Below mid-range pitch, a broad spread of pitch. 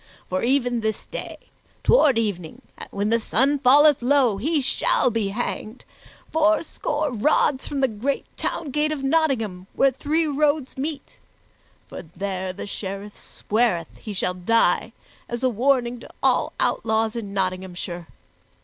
No: high, 240 Hz; wide, 5.9 semitones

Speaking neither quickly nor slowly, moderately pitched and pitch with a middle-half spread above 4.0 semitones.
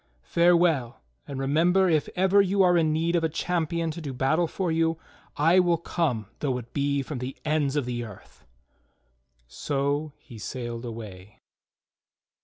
Yes: average, 160 wpm; medium, 150 Hz; average, 4.9 semitones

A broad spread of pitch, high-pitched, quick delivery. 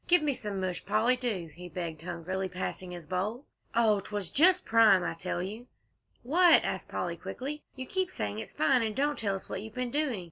Yes: wide, 5.9 semitones; high, 210 Hz; fast, 210 wpm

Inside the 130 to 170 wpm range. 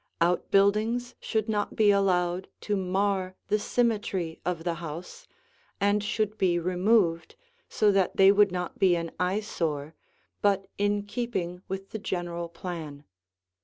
Yes: average, 140 wpm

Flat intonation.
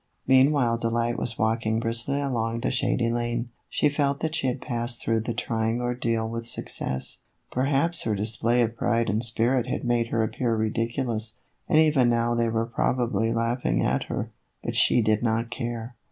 Yes: narrow, 1.5 semitones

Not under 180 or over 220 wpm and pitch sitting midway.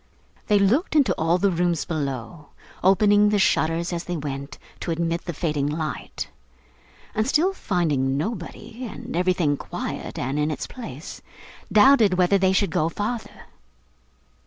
No: average, 145 wpm; medium, 175 Hz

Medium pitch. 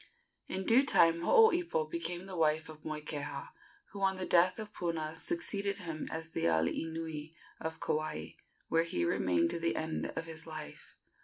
Yes: medium, 165 Hz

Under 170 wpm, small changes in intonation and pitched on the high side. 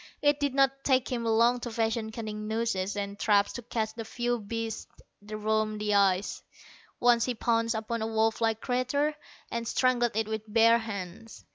No: average, 180 wpm; narrow, 1.9 semitones; high, 225 Hz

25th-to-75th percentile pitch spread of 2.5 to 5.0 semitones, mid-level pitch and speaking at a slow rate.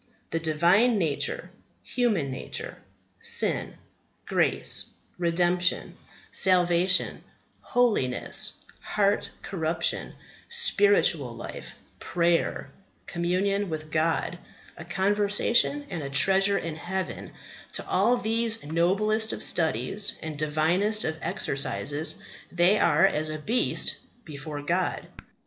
Yes: average, 4.5 semitones; medium, 175 Hz; slow, 100 wpm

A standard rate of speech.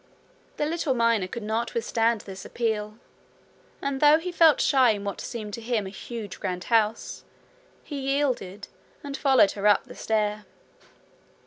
Yes: average, 155 wpm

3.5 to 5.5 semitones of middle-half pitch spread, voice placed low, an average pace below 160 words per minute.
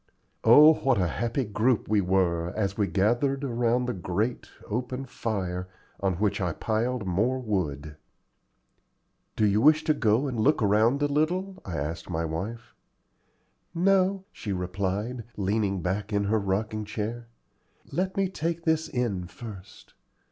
Yes: average, 5.2 semitones; low, 110 Hz; average, 150 wpm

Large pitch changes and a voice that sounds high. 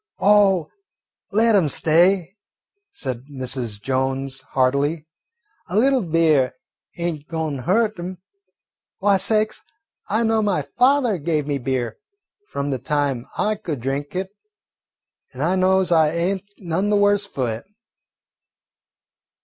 No: wide, 6.4 semitones; medium, 165 Hz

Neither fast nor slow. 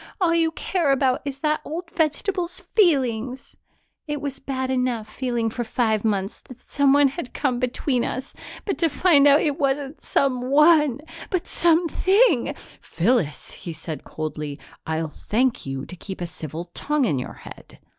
Yes: average, 160 wpm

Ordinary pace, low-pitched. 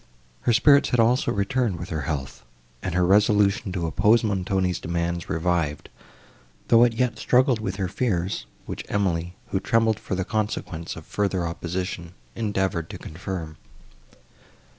Yes: average, 145 wpm; very low, 95 Hz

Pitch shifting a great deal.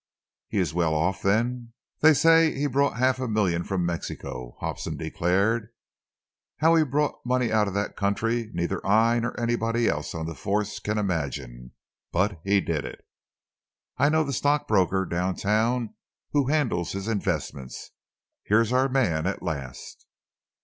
Yes: wide, 6.1 semitones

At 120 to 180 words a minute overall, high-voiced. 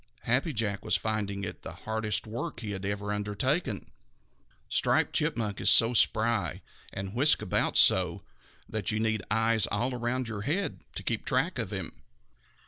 No: average, 160 wpm; low, 110 Hz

